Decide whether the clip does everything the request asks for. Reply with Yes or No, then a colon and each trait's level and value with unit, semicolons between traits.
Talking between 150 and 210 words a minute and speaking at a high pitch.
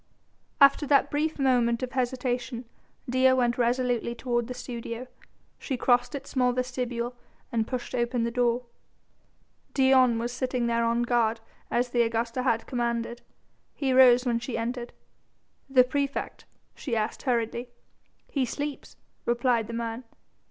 No: average, 140 wpm; high, 245 Hz